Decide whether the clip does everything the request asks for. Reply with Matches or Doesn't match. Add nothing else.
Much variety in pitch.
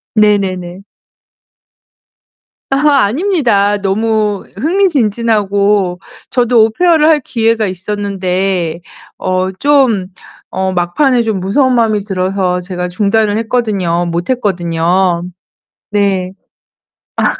Doesn't match